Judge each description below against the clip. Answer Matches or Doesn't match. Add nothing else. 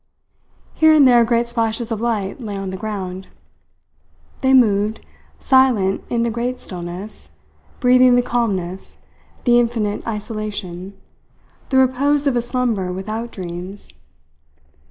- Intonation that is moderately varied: Matches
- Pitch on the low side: Doesn't match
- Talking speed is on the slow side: Matches